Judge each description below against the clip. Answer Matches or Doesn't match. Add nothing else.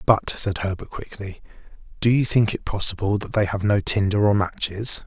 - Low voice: Matches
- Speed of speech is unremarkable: Matches